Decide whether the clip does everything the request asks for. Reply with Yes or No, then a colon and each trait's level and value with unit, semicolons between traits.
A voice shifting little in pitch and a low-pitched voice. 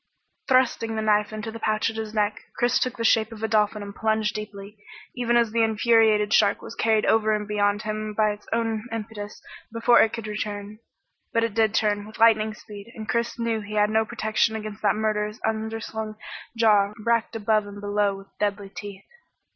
No: narrow, 1.2 semitones; high, 215 Hz